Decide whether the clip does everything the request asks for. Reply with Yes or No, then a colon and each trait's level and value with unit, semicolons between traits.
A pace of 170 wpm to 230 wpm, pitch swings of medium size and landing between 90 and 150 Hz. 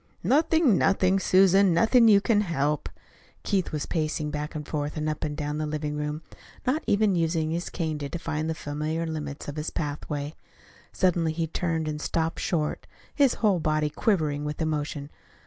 No: average, 175 wpm; average, 3.5 semitones; medium, 160 Hz